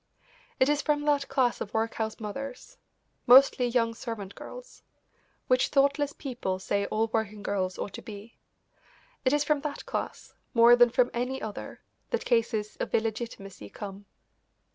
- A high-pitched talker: Yes, high, 235 Hz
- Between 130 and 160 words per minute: Yes, average, 150 wpm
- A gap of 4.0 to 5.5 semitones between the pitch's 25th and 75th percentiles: Yes, average, 4.4 semitones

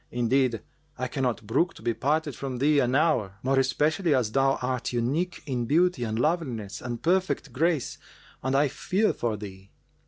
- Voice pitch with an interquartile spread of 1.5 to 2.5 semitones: No, average, 4.2 semitones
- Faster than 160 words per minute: Yes, average, 175 wpm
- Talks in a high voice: No, low, 130 Hz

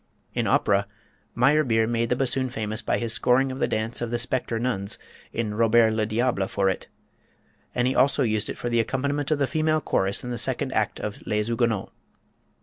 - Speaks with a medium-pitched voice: No, low, 120 Hz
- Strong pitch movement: No, average, 3.0 semitones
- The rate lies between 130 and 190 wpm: No, average, 200 wpm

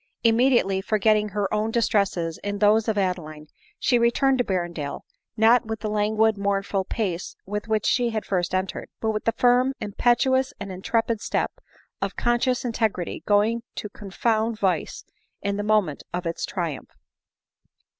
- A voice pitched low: No, high, 210 Hz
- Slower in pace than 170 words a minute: Yes, average, 155 wpm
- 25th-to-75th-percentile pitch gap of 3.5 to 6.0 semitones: No, average, 3.0 semitones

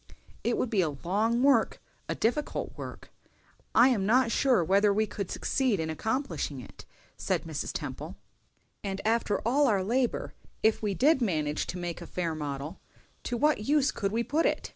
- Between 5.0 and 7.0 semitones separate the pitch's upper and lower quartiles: Yes, wide, 5.4 semitones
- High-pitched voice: Yes, high, 215 Hz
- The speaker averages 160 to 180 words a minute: Yes, average, 175 wpm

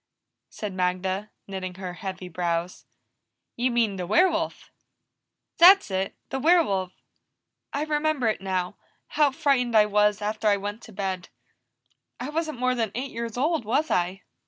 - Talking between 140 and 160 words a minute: Yes, average, 150 wpm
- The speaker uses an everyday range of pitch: No, wide, 5.8 semitones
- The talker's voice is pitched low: No, high, 210 Hz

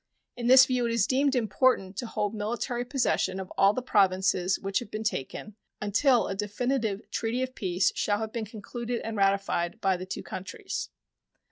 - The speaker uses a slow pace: No, average, 180 wpm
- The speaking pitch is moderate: No, high, 215 Hz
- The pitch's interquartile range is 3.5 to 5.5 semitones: Yes, average, 3.8 semitones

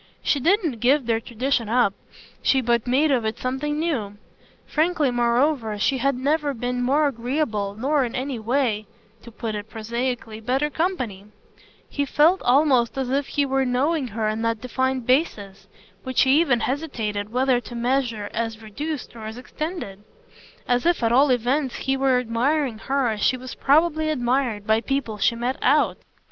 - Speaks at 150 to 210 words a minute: Yes, average, 170 wpm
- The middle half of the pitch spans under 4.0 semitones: Yes, average, 3.6 semitones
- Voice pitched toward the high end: Yes, very high, 250 Hz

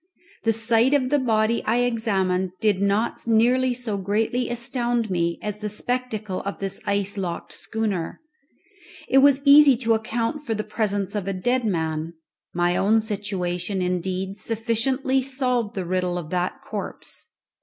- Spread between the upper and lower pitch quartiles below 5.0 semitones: Yes, average, 4.2 semitones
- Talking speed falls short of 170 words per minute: Yes, average, 155 wpm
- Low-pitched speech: No, high, 215 Hz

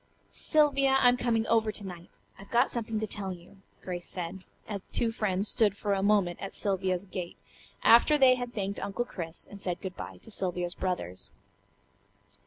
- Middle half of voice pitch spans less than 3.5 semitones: No, average, 3.9 semitones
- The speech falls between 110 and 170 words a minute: No, average, 185 wpm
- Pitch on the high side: Yes, high, 200 Hz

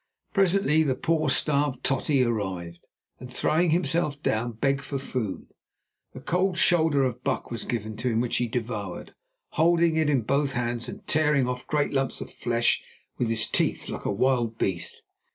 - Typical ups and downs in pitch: Yes, average, 4.5 semitones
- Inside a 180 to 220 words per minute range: No, average, 170 wpm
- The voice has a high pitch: No, low, 130 Hz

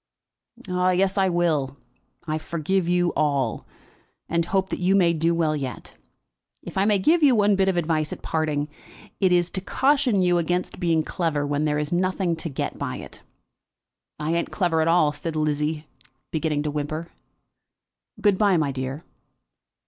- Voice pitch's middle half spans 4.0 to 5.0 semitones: No, average, 3.4 semitones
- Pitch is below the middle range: No, medium, 170 Hz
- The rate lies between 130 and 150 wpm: No, average, 165 wpm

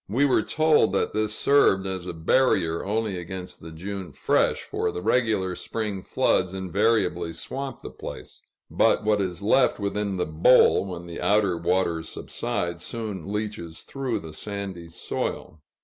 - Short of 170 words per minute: Yes, average, 155 wpm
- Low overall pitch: Yes, very low, 95 Hz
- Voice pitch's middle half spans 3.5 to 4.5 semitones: Yes, average, 3.8 semitones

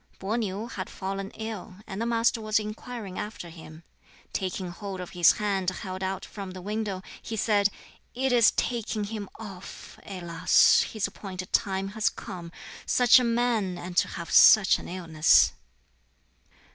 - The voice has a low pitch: No, high, 195 Hz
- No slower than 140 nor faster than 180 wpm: Yes, average, 160 wpm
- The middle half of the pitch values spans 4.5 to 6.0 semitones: No, average, 3.0 semitones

